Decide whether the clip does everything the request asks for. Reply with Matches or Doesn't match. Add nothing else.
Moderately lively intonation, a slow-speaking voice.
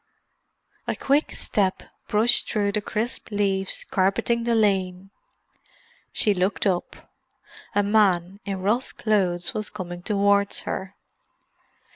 Doesn't match